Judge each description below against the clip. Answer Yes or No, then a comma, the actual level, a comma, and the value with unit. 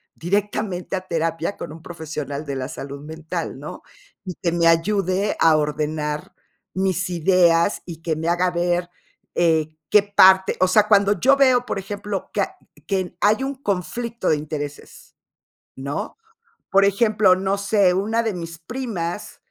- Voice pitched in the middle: Yes, medium, 180 Hz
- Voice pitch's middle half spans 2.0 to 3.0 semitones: No, average, 3.9 semitones